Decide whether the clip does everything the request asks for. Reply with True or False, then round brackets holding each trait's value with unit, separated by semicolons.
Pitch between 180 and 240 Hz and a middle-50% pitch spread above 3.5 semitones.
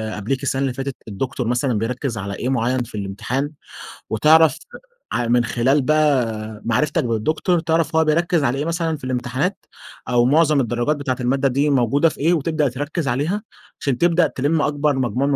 False (135 Hz; 4.0 semitones)